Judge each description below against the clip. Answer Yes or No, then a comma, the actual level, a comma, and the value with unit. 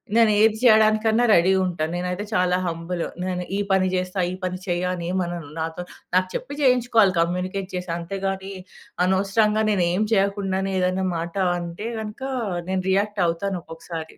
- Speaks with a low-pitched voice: No, medium, 185 Hz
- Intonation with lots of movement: No, narrow, 2.5 semitones